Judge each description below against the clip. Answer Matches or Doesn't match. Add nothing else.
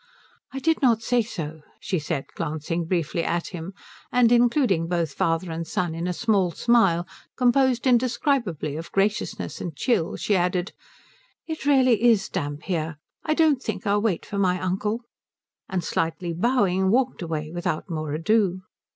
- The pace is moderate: Matches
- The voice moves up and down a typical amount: Doesn't match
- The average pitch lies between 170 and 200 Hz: Matches